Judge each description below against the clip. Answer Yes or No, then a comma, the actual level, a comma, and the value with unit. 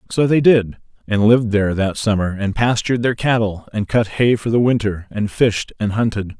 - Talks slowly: No, fast, 205 wpm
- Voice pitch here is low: Yes, low, 110 Hz